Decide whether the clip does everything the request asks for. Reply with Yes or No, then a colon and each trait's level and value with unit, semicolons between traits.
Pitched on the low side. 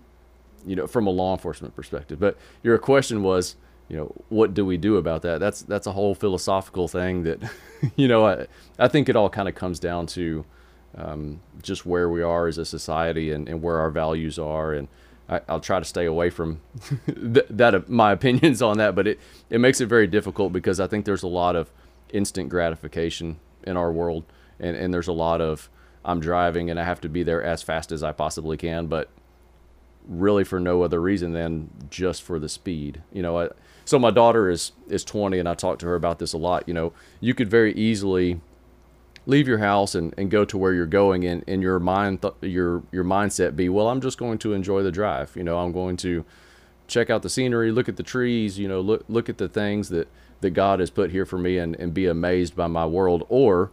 Yes: very low, 90 Hz